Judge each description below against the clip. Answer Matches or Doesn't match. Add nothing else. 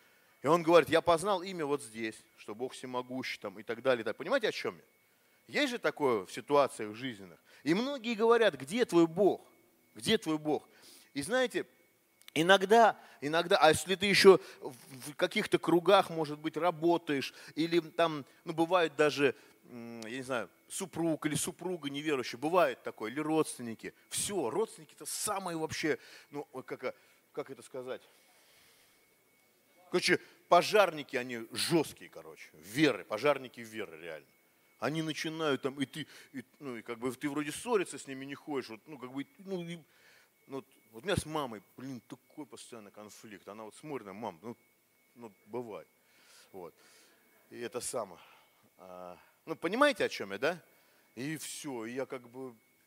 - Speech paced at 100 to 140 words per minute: Doesn't match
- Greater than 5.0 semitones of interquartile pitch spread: Matches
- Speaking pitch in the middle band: Matches